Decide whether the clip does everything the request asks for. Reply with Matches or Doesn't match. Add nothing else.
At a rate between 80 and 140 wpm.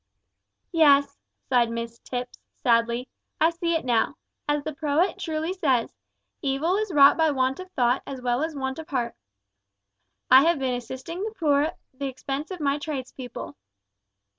Doesn't match